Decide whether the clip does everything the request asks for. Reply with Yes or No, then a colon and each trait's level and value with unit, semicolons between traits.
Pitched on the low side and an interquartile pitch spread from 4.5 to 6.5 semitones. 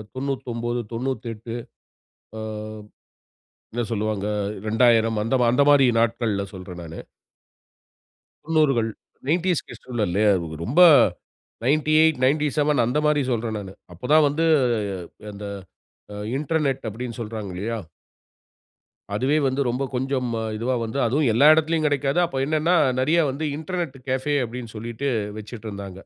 Yes: low, 125 Hz; average, 4.8 semitones